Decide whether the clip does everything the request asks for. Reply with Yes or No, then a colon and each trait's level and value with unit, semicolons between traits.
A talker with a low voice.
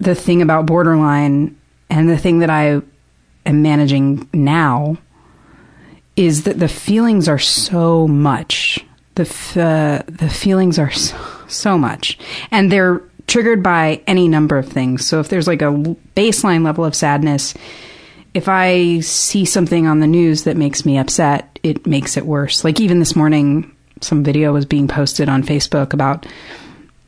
No: medium, 155 Hz